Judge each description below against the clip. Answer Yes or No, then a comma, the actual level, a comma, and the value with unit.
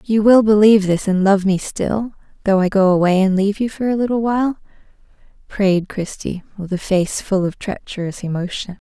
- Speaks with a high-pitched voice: Yes, high, 200 Hz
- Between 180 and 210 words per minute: Yes, average, 190 wpm